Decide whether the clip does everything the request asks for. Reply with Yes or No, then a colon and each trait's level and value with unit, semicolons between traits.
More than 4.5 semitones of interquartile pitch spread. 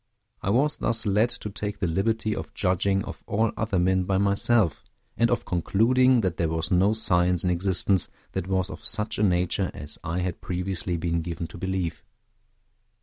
No: average, 3.3 semitones